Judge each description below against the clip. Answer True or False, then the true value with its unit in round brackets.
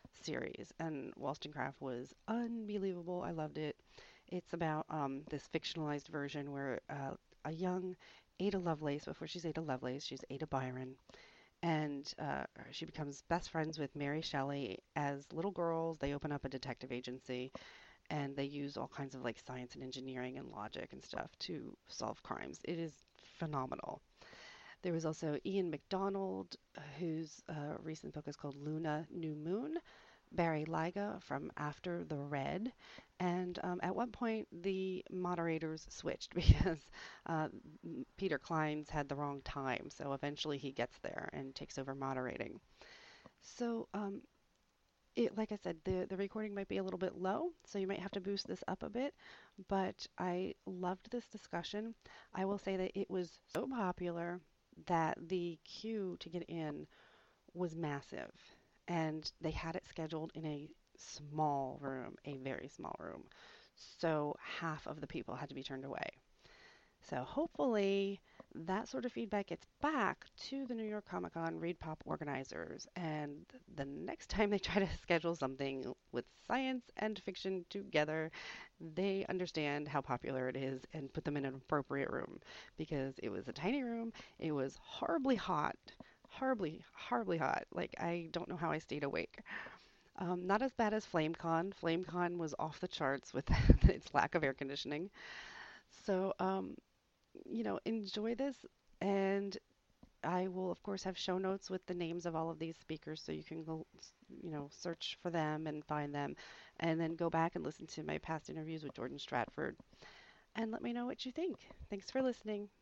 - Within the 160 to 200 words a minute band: True (170 wpm)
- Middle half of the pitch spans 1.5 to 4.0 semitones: False (4.8 semitones)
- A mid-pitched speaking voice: True (165 Hz)